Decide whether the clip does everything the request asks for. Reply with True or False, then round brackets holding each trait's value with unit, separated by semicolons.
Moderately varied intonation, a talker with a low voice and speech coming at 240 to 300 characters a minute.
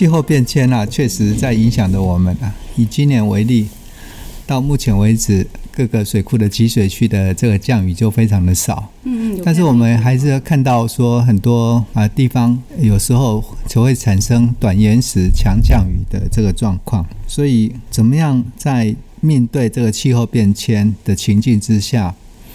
True (3.1 semitones; 115 Hz; 255 characters per minute)